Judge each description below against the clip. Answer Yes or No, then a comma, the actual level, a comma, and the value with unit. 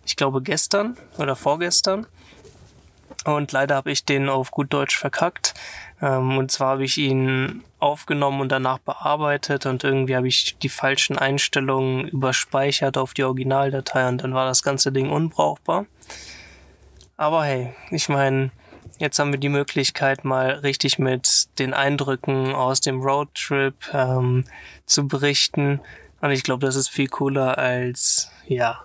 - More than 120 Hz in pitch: Yes, low, 135 Hz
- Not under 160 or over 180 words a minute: No, average, 145 wpm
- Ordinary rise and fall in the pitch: No, narrow, 1.3 semitones